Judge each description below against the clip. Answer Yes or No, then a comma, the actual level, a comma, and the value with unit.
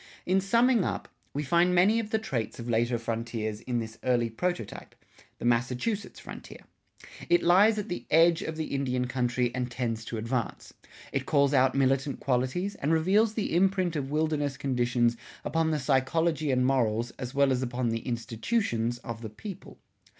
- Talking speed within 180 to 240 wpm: No, average, 170 wpm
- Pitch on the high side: No, low, 135 Hz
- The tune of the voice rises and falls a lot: Yes, wide, 6.0 semitones